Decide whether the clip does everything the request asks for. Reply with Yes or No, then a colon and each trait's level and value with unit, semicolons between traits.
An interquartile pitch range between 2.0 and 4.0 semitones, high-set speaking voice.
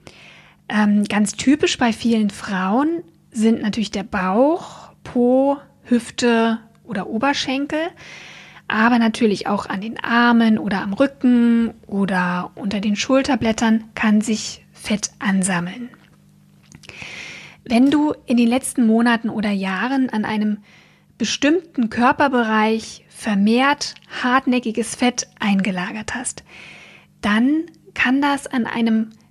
Yes: average, 3.4 semitones; high, 230 Hz